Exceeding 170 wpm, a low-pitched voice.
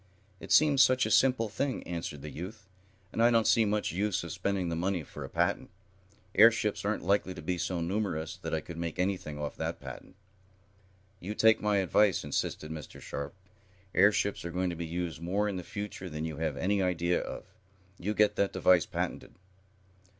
Yes: average, 195 wpm; very low, 95 Hz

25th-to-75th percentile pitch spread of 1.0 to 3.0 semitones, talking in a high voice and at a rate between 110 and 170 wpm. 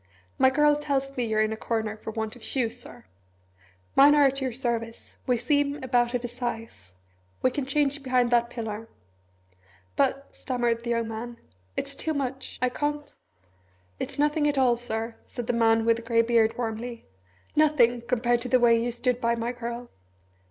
No: narrow, 2.6 semitones; high, 240 Hz; average, 185 wpm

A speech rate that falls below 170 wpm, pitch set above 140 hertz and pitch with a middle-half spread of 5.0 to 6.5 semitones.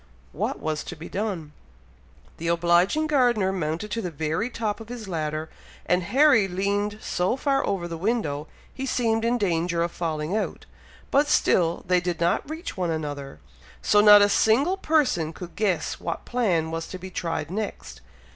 No: average, 175 wpm; medium, 185 Hz; average, 5.3 semitones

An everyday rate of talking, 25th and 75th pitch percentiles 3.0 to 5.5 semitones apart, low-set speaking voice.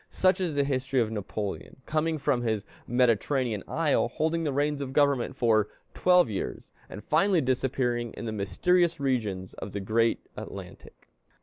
Yes: average, 160 wpm; average, 5.1 semitones; low, 130 Hz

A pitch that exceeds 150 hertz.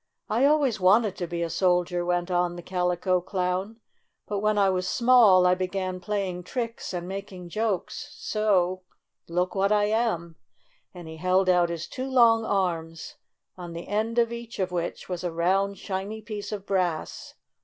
Yes: medium, 185 Hz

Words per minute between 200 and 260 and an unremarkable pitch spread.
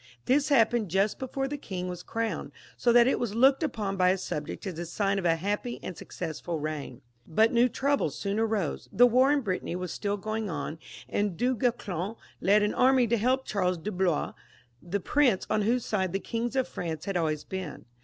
Yes: fast, 205 wpm; average, 5.0 semitones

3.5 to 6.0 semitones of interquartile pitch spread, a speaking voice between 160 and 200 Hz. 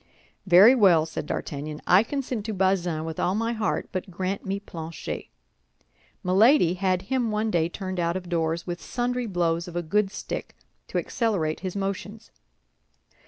Yes: average, 3.8 semitones; medium, 185 Hz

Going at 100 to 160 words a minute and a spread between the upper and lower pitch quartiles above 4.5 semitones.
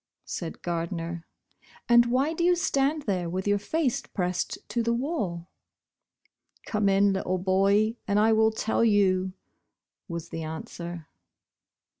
Yes: average, 140 wpm; average, 4.9 semitones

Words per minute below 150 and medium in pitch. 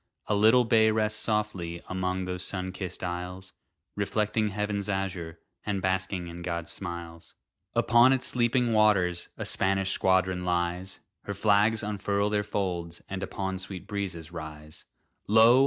No: average, 140 wpm; very low, 95 Hz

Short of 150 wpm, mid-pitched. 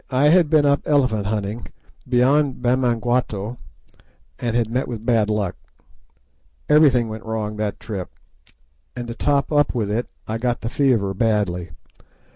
No: average, 140 wpm; low, 120 Hz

